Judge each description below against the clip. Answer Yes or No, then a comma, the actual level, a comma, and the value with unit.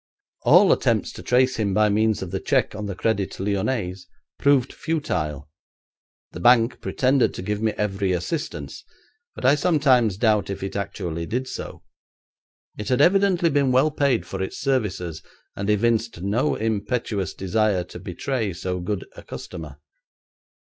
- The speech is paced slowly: No, average, 155 wpm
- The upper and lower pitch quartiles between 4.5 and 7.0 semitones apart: Yes, average, 5.2 semitones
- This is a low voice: Yes, low, 105 Hz